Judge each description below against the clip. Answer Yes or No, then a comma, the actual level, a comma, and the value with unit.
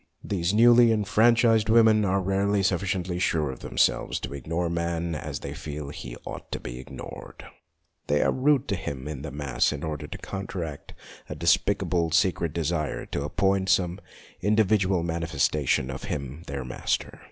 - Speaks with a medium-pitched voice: No, very low, 85 Hz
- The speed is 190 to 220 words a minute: No, average, 165 wpm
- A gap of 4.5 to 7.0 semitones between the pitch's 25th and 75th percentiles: Yes, average, 5.0 semitones